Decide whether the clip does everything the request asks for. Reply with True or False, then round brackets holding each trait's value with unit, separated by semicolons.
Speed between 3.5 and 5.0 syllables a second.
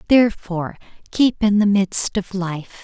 True (4.6 syllables/s)